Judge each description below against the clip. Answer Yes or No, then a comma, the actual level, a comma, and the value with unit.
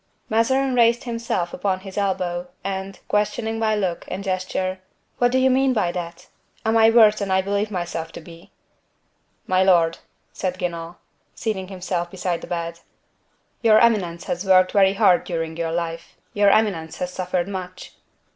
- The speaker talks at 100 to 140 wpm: No, average, 165 wpm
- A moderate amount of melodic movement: Yes, average, 3.5 semitones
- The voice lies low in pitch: No, high, 190 Hz